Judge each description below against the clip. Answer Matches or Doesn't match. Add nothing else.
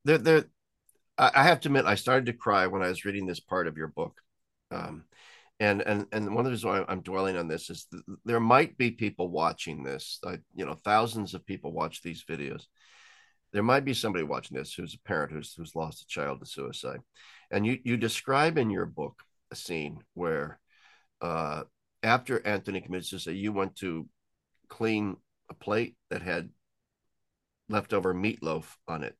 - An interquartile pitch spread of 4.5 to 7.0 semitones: Doesn't match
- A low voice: Matches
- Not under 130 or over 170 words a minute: Doesn't match